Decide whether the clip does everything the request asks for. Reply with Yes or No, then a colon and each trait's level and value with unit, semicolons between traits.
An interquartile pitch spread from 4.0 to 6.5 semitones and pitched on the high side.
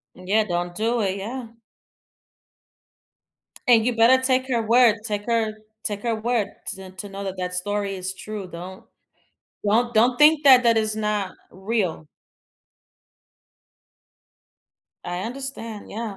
No: average, 3.6 semitones; high, 215 Hz